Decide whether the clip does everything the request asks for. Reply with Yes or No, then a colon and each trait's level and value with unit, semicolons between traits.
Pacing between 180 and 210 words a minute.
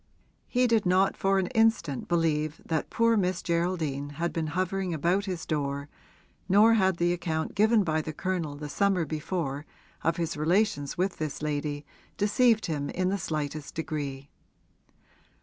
No: average, 155 wpm